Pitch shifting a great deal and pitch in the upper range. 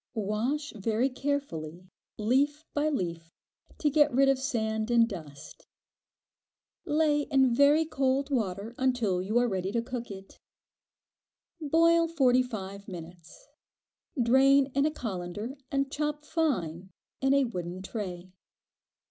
Yes: wide, 6.6 semitones; high, 245 Hz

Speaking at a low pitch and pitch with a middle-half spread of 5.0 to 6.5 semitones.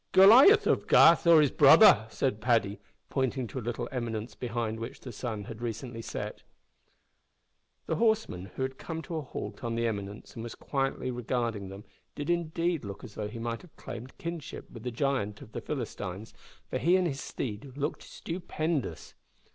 Yes: low, 125 Hz; wide, 5.4 semitones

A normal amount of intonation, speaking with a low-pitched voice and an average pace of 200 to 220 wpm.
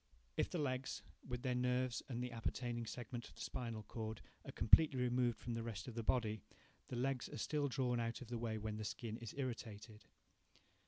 No: narrow, 2.0 semitones; low, 120 Hz; fast, 205 wpm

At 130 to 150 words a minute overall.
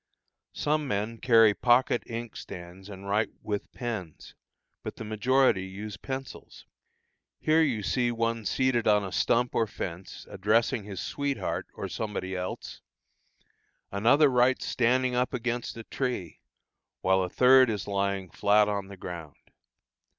Yes: average, 140 wpm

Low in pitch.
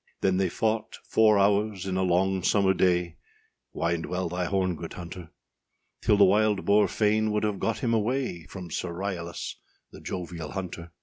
Yes: very low, 95 Hz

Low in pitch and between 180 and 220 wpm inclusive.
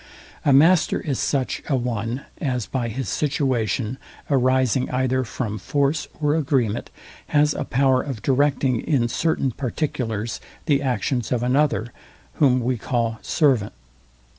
No: low, 130 Hz; slow, 135 wpm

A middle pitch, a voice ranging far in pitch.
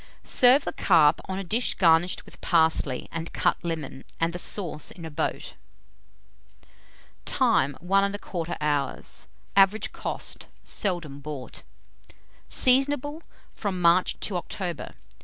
No: medium, 175 Hz; average, 3.7 semitones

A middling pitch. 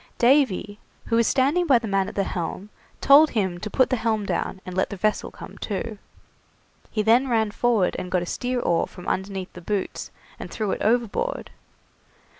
No: high, 215 Hz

